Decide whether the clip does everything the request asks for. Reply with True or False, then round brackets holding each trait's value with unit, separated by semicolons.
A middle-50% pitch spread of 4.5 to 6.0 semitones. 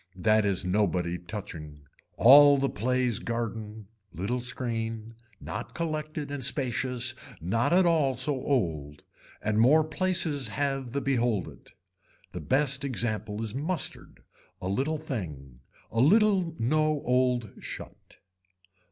True (5.0 semitones)